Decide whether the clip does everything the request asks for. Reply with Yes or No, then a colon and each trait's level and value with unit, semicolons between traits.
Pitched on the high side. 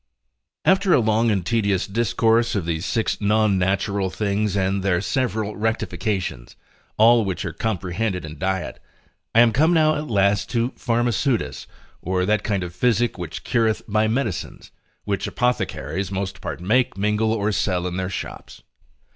No: low, 105 Hz